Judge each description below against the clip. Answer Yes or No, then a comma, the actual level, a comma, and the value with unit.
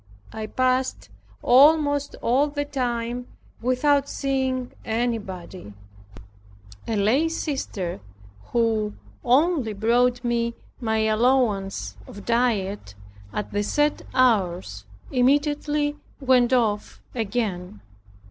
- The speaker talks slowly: Yes, slow, 90 wpm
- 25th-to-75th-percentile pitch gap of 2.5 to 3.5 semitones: No, average, 4.2 semitones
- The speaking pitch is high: Yes, high, 240 Hz